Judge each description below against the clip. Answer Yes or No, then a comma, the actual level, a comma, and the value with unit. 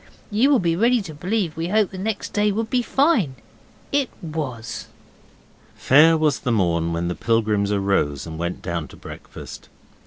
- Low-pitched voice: No, medium, 155 Hz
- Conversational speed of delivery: Yes, average, 165 wpm